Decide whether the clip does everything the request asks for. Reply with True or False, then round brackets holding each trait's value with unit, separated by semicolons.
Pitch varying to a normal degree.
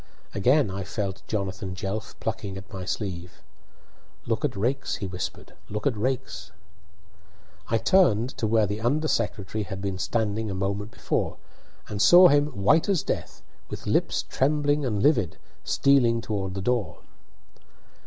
True (4.8 semitones)